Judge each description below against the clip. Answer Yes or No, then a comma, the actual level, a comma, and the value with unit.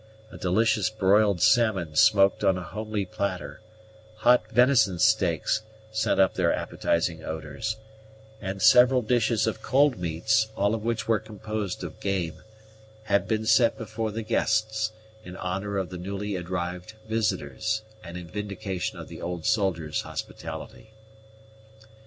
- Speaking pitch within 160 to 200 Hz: No, low, 105 Hz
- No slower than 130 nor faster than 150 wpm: Yes, average, 140 wpm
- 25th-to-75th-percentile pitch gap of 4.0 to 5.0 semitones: No, average, 3.2 semitones